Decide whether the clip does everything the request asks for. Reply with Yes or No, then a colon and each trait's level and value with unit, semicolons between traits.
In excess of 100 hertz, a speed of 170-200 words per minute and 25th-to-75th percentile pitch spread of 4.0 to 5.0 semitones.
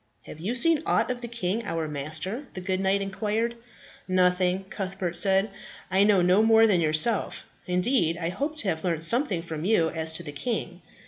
Yes: high, 190 Hz; average, 190 wpm; average, 4.7 semitones